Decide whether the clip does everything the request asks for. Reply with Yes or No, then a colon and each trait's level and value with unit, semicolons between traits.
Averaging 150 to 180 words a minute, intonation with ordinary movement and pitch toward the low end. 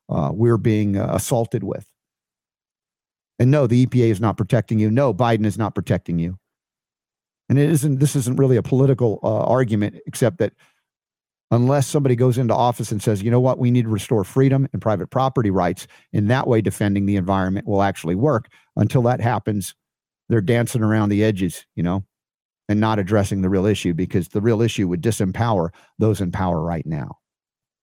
No: average, 190 wpm; average, 3.8 semitones; low, 110 Hz